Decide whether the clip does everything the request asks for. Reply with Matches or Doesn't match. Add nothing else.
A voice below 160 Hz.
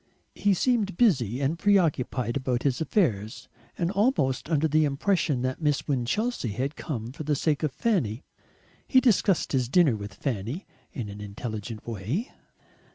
Matches